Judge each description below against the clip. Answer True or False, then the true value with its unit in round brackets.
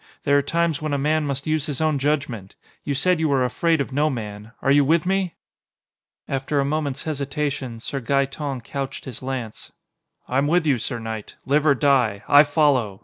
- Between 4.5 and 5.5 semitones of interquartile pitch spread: False (2.7 semitones)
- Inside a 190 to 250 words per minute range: True (195 wpm)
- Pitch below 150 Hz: True (140 Hz)